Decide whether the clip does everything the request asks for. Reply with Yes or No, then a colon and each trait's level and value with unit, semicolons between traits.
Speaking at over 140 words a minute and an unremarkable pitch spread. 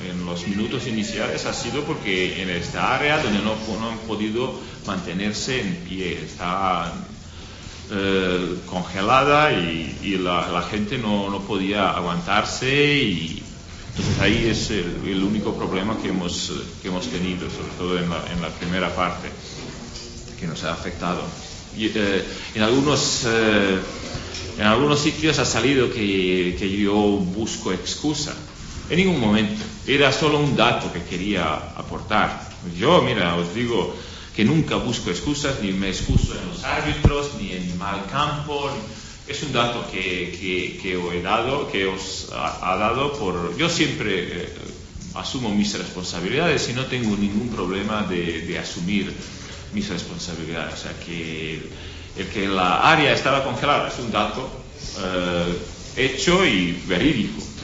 Yes: average, 150 wpm; average, 3.7 semitones